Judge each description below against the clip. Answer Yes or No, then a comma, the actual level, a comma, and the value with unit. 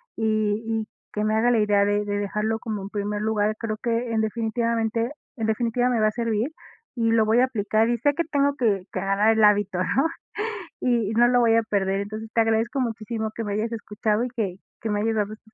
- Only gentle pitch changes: Yes, narrow, 1.8 semitones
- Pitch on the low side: No, high, 220 Hz